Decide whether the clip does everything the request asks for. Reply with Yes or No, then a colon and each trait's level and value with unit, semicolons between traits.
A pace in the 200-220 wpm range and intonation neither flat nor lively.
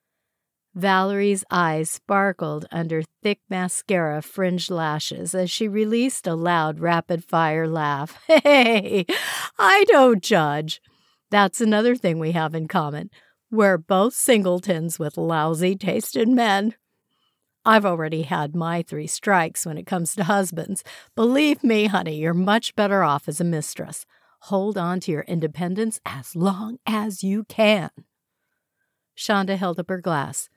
No: slow, 135 wpm; average, 4.4 semitones